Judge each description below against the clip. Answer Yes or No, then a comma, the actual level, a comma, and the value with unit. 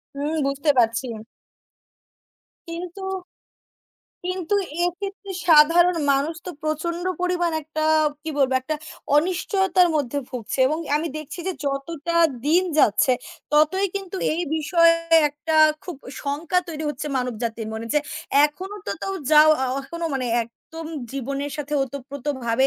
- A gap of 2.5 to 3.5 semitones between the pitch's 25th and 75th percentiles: No, average, 4.0 semitones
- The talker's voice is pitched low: No, very high, 310 Hz